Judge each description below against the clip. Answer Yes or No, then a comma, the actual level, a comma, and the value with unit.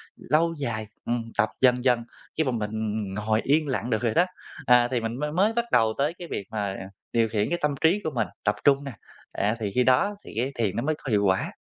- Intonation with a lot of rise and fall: No, average, 5.0 semitones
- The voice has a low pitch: Yes, low, 125 Hz